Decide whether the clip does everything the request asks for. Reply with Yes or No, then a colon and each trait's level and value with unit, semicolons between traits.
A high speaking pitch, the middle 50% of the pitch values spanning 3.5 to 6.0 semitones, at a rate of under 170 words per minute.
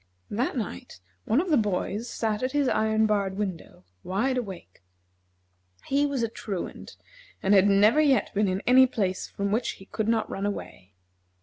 No: high, 215 Hz; average, 4.3 semitones; average, 175 wpm